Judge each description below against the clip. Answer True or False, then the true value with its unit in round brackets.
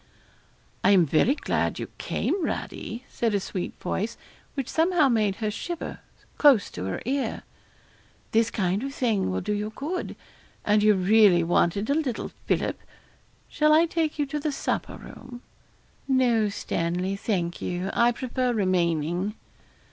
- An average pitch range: False (6.4 semitones)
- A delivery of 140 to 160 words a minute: True (150 wpm)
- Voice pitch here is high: True (220 Hz)